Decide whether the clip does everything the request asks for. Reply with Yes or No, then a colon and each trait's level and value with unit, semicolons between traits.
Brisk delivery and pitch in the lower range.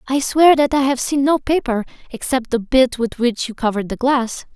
No: fast, 225 wpm; very high, 255 Hz